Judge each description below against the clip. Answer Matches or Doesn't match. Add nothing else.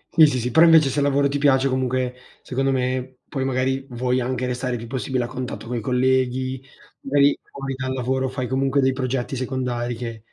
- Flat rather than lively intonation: Matches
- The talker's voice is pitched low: Matches